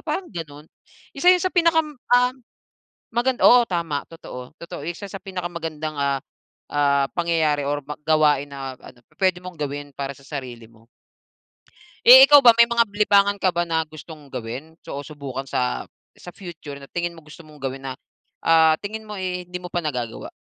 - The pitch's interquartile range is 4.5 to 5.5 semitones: Yes, average, 5.1 semitones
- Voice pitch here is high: No, medium, 160 Hz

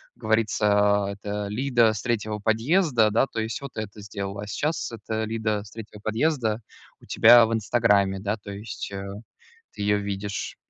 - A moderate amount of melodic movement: No, narrow, 2.0 semitones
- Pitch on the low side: Yes, low, 110 Hz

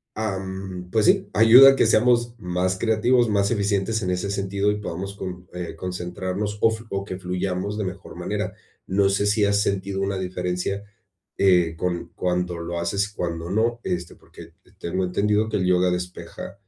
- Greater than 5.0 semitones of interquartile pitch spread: No, narrow, 2.4 semitones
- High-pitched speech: No, very low, 95 Hz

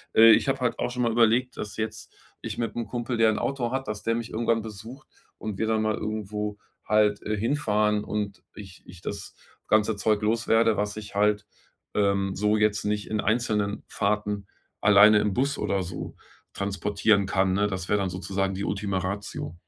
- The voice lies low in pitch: Yes, low, 105 Hz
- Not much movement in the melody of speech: Yes, narrow, 1.9 semitones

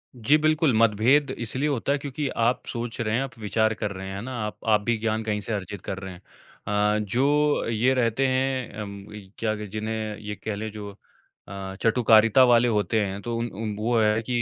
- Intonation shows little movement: No, average, 3.1 semitones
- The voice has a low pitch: Yes, low, 110 Hz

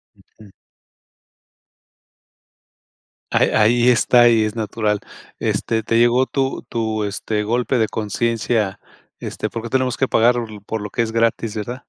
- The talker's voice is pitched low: Yes, low, 115 Hz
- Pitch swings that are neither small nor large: No, narrow, 1.9 semitones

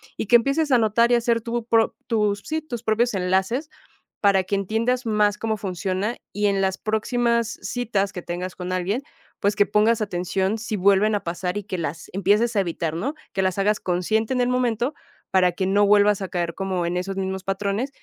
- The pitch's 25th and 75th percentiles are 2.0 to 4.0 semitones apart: Yes, average, 3.5 semitones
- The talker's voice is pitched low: No, high, 205 Hz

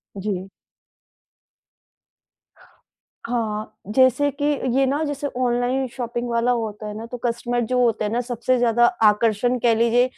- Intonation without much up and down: Yes, narrow, 1.9 semitones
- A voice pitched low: No, high, 240 Hz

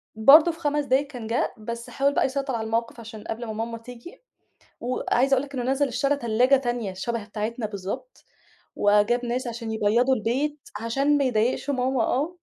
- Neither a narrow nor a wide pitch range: Yes, average, 3.4 semitones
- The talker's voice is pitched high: Yes, high, 245 Hz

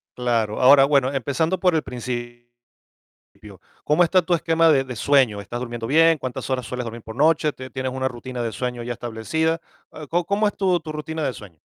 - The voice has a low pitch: Yes, low, 130 Hz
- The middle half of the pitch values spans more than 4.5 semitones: Yes, average, 4.9 semitones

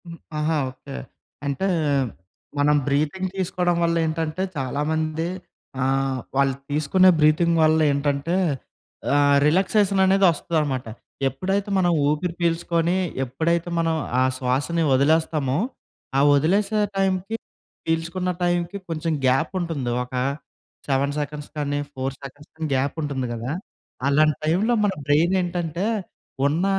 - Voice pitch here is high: No, medium, 160 Hz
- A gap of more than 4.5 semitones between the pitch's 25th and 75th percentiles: No, average, 3.6 semitones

